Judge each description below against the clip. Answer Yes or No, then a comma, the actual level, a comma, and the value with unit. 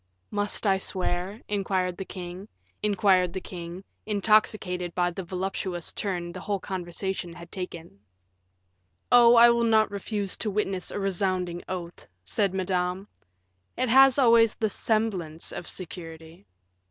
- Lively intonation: No, average, 2.8 semitones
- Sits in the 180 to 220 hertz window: Yes, high, 190 Hz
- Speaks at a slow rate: Yes, slow, 125 wpm